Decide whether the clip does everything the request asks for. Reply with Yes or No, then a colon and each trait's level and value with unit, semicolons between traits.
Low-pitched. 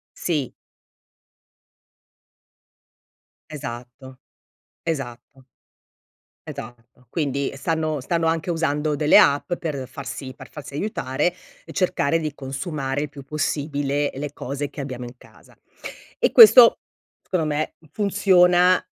No: medium, 145 Hz